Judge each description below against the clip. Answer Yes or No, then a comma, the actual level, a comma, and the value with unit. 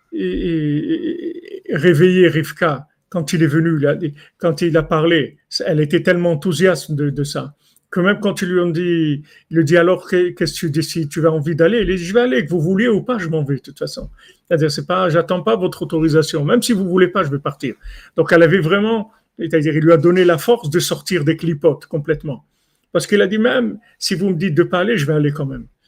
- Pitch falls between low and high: Yes, medium, 170 Hz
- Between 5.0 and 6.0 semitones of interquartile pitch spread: No, average, 2.9 semitones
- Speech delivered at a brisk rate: Yes, fast, 235 wpm